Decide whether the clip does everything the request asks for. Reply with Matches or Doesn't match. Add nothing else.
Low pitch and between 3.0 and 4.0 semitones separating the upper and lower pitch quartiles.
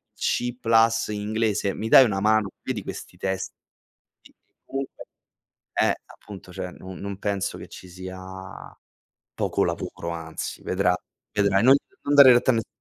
Matches